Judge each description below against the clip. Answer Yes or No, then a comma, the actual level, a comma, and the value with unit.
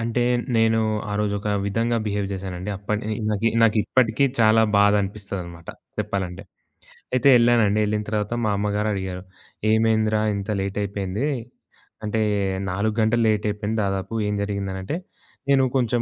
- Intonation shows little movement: Yes, narrow, 2.1 semitones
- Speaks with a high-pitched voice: No, low, 105 Hz